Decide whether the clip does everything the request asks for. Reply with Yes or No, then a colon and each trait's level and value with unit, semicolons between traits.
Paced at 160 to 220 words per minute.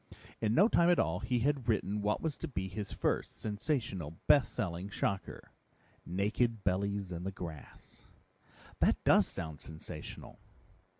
No: average, 145 wpm